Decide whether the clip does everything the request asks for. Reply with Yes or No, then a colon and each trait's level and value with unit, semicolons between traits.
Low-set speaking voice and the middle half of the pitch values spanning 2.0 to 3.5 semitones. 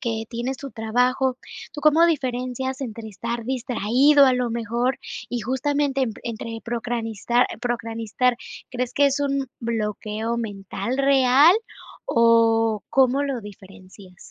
No: high, 245 Hz; average, 2.9 semitones